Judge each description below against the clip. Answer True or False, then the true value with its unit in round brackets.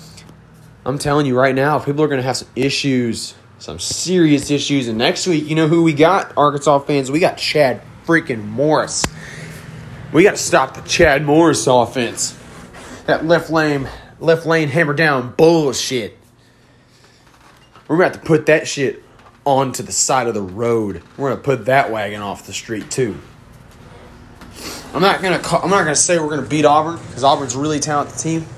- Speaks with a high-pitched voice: False (140 Hz)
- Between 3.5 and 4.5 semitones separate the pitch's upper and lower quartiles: True (4.2 semitones)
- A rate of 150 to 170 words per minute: False (180 wpm)